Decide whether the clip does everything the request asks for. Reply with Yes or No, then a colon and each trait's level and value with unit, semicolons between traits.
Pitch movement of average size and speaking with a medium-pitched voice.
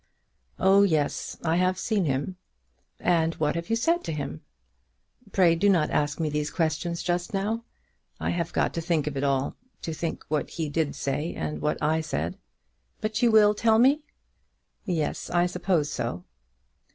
Yes: average, 4.4 semitones; medium, 170 Hz